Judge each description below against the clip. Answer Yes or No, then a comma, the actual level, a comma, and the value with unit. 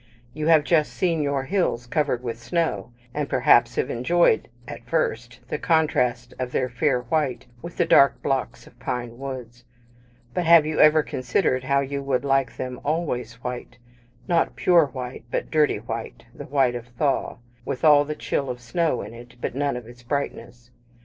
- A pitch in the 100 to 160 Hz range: Yes, low, 135 Hz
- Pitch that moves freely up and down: No, average, 3.8 semitones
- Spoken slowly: No, average, 180 wpm